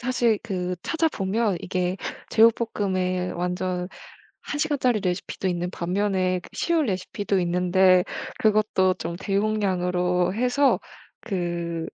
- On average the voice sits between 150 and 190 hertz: Yes, medium, 185 Hz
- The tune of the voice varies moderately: Yes, average, 3.1 semitones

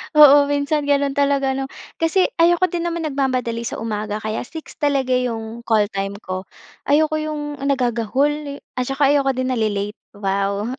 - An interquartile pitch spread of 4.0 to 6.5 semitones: Yes, average, 4.5 semitones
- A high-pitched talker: Yes, very high, 270 Hz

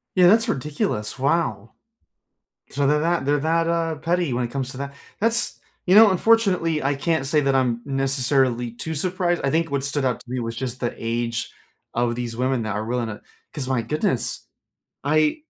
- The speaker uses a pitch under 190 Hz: Yes, medium, 140 Hz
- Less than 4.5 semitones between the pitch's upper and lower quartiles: No, average, 5.2 semitones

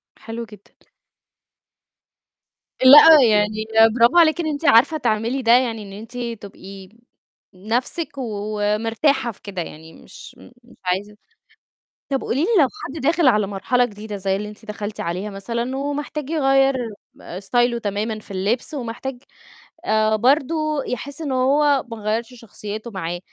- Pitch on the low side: No, high, 230 Hz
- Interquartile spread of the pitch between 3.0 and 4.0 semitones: No, average, 4.5 semitones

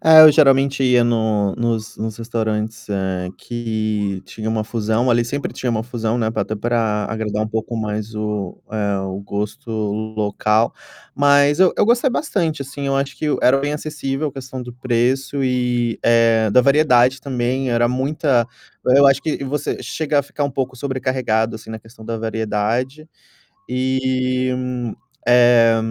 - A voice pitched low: Yes, low, 120 Hz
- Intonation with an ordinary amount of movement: Yes, average, 3.5 semitones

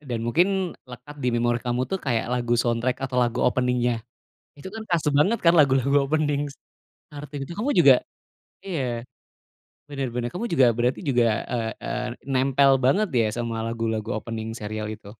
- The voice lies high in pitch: No, low, 125 Hz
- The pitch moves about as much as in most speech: Yes, average, 3.7 semitones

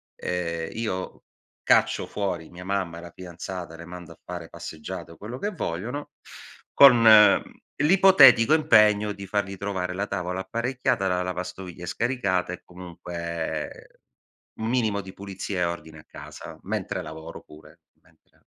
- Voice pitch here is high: No, very low, 95 Hz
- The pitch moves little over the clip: No, average, 3.7 semitones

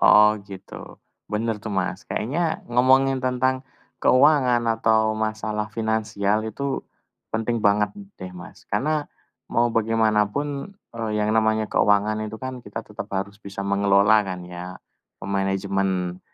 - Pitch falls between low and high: No, low, 110 Hz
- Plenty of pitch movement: No, average, 2.9 semitones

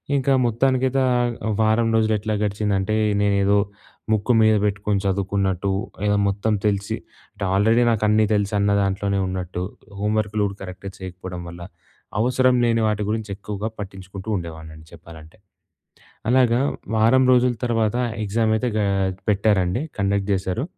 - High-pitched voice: No, low, 105 Hz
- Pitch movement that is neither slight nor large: No, narrow, 2.3 semitones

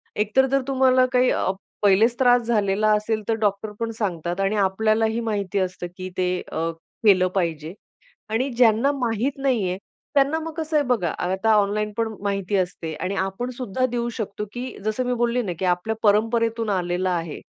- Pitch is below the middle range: No, high, 215 Hz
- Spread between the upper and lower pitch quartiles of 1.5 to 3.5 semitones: No, average, 4.2 semitones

